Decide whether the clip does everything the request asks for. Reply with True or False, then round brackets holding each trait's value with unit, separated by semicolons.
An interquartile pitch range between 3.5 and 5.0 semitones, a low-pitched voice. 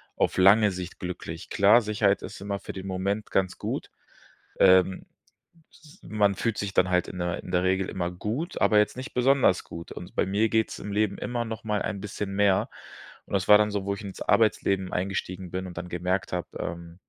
False (2.4 semitones; 100 Hz)